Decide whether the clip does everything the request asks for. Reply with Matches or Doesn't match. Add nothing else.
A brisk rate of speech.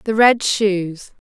Doesn't match